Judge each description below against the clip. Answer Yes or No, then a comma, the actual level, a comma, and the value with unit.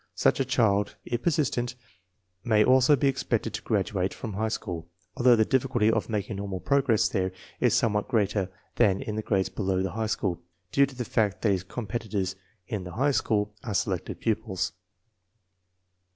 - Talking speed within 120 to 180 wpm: Yes, average, 175 wpm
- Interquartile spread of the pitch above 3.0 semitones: Yes, average, 3.8 semitones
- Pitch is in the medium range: No, low, 110 Hz